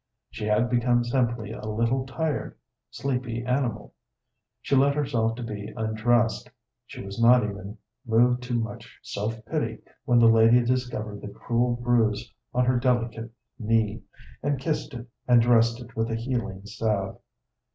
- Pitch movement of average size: No, narrow, 1.8 semitones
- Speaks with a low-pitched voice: Yes, low, 115 Hz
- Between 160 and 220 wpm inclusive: No, average, 150 wpm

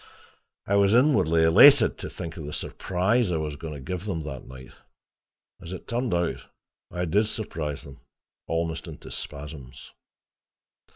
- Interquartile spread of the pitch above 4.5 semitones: Yes, average, 4.9 semitones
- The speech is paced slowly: No, average, 155 wpm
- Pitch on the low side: Yes, very low, 85 Hz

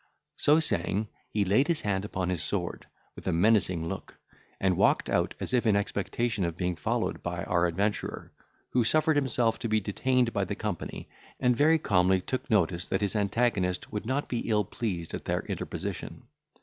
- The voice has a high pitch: No, low, 105 Hz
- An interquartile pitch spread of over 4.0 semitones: Yes, average, 4.6 semitones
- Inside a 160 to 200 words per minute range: Yes, average, 185 wpm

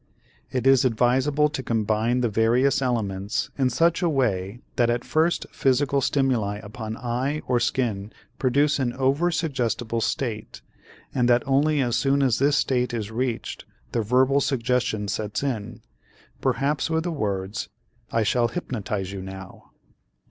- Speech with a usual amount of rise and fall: Yes, average, 3.7 semitones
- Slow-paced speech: No, average, 150 wpm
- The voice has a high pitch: No, low, 125 Hz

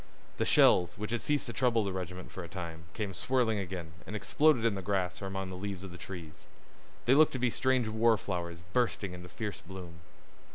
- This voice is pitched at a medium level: No, very low, 95 Hz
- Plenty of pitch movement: No, average, 4.3 semitones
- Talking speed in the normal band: No, fast, 215 wpm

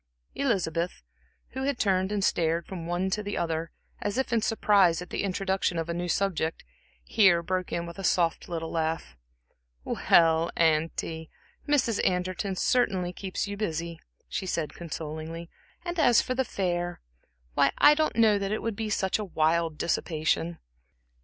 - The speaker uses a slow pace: No, average, 160 wpm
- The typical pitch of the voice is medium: Yes, medium, 180 Hz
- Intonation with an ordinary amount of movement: Yes, average, 3.7 semitones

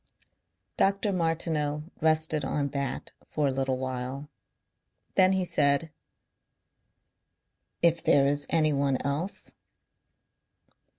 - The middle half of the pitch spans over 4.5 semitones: No, average, 2.9 semitones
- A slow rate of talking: Yes, slow, 95 wpm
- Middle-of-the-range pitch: Yes, medium, 150 Hz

